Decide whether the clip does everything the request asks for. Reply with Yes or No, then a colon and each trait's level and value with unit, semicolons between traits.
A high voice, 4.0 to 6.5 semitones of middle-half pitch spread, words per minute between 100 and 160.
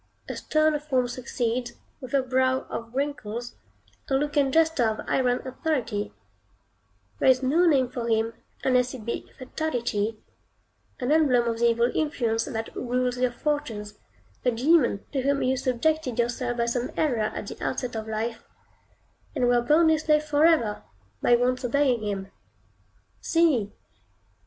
No: very high, 250 Hz; average, 3.5 semitones; average, 150 wpm